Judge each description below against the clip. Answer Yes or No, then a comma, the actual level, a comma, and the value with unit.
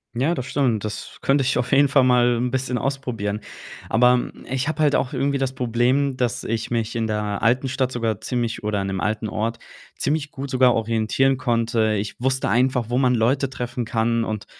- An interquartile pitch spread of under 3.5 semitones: Yes, average, 2.8 semitones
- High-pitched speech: No, low, 125 Hz